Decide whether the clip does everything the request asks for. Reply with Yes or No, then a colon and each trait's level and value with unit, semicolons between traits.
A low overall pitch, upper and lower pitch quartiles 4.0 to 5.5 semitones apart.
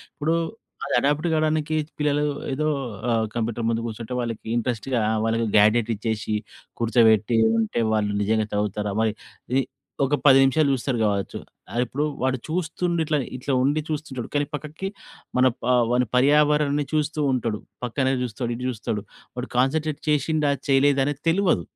Yes: low, 130 Hz; average, 4.6 semitones